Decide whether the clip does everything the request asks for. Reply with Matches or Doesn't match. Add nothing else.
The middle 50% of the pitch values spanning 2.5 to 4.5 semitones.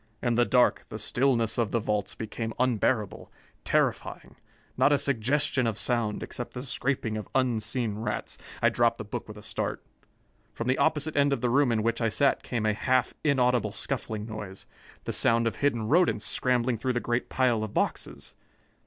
Matches